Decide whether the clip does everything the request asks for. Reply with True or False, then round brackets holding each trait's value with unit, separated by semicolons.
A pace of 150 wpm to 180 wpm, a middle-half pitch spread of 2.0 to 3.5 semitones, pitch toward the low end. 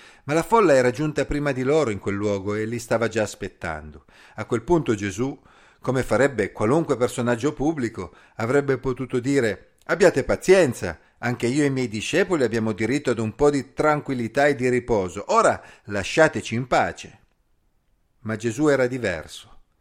False (165 wpm; 4.7 semitones; 125 Hz)